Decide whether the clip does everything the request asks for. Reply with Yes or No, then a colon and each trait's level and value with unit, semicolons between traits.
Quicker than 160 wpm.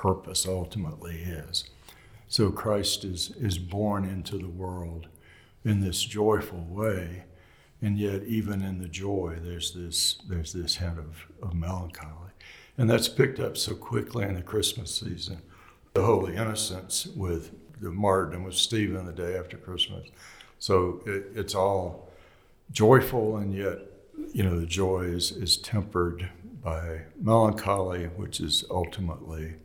No: average, 140 wpm